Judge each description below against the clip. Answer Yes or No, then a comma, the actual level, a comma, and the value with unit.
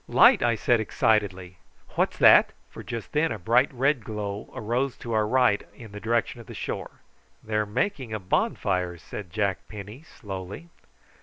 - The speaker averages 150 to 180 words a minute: Yes, average, 170 wpm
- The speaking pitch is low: Yes, low, 110 Hz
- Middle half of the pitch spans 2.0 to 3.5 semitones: Yes, average, 3.2 semitones